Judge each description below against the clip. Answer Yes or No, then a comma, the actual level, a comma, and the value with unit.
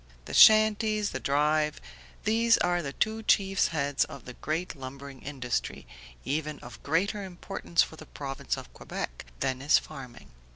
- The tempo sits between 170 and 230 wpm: No, average, 155 wpm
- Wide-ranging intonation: Yes, wide, 6.2 semitones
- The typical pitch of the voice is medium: Yes, medium, 155 Hz